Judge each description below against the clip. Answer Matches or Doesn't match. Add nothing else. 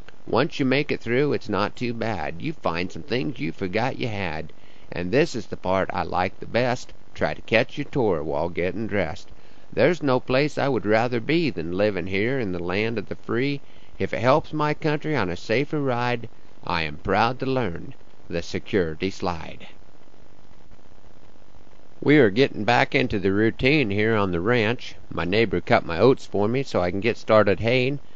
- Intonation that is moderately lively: Doesn't match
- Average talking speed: Matches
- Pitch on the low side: Matches